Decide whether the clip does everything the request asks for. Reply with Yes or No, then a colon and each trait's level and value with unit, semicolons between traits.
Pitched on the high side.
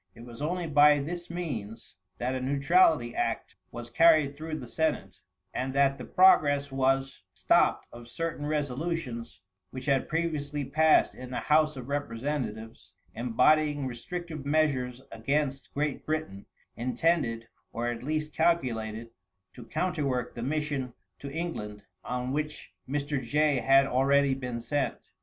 No: medium, 140 Hz